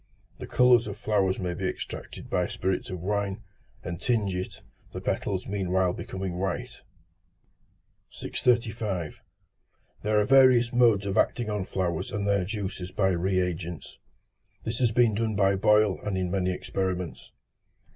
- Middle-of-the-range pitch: No, low, 100 Hz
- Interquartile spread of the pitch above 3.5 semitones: No, average, 2.9 semitones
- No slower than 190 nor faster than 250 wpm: No, average, 145 wpm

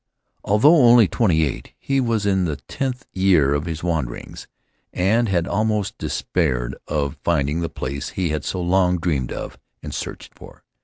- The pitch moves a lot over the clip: Yes, wide, 5.8 semitones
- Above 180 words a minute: No, average, 165 wpm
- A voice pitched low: Yes, very low, 90 Hz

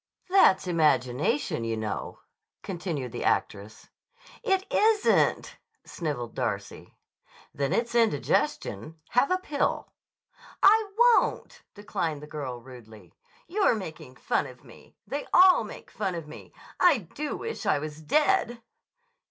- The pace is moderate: No, slow, 125 wpm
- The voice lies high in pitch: No, medium, 170 Hz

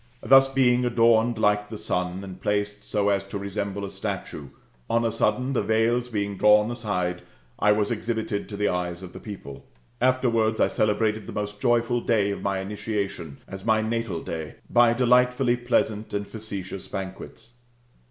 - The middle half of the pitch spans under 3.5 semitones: Yes, average, 2.8 semitones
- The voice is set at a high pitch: No, low, 105 Hz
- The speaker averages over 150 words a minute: Yes, average, 170 wpm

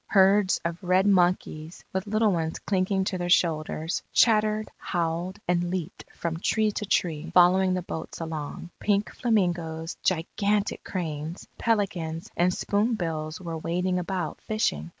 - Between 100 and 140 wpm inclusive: Yes, slow, 135 wpm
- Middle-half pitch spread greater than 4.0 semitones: No, average, 3.4 semitones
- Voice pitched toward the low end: No, medium, 180 Hz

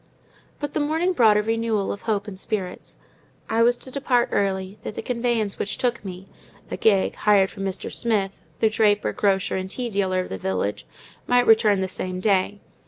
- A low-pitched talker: No, high, 210 Hz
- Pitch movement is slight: No, average, 3.4 semitones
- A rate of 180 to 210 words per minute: Yes, average, 190 wpm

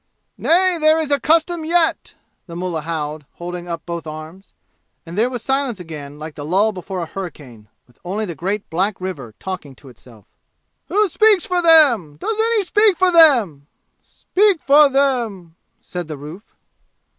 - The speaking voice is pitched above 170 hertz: Yes, high, 190 Hz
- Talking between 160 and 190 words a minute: Yes, average, 170 wpm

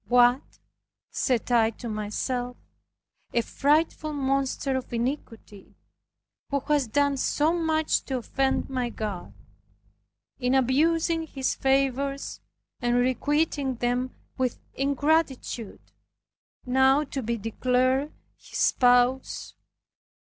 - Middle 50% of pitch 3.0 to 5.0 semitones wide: No, narrow, 2.6 semitones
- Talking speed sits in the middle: No, slow, 100 wpm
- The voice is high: Yes, very high, 265 Hz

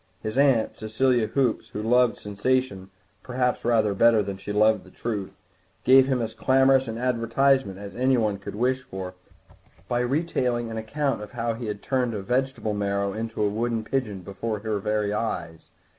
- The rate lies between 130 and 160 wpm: No, average, 175 wpm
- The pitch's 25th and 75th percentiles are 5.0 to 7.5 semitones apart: No, average, 3.5 semitones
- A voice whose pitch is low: Yes, low, 115 Hz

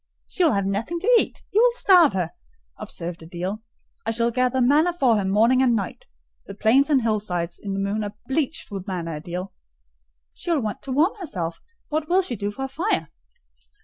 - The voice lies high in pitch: Yes, high, 230 Hz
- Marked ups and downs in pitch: Yes, wide, 7.3 semitones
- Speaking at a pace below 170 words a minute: No, average, 200 wpm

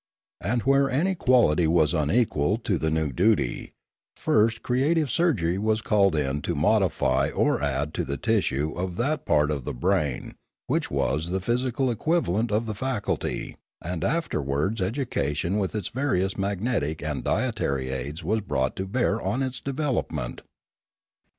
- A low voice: Yes, very low, 95 Hz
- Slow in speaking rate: No, average, 150 wpm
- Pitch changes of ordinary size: No, wide, 8.0 semitones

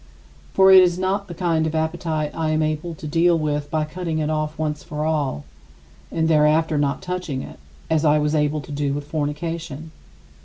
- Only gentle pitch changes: Yes, narrow, 1.8 semitones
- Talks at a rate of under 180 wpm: No, average, 195 wpm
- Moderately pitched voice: Yes, medium, 155 Hz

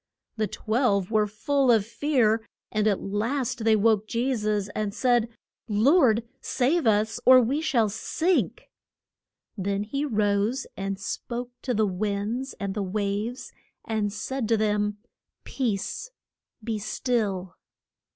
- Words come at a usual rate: No, slow, 130 wpm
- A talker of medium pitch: No, high, 220 Hz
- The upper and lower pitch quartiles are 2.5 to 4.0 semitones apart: Yes, average, 3.2 semitones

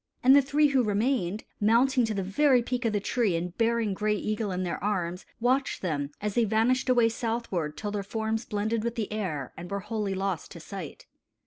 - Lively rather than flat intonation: No, average, 3.5 semitones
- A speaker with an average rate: No, fast, 210 wpm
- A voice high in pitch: Yes, high, 215 Hz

